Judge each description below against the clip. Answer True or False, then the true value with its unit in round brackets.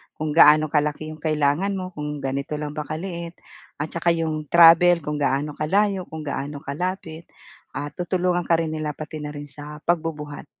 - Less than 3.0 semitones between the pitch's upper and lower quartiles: True (2.4 semitones)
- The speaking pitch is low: False (155 Hz)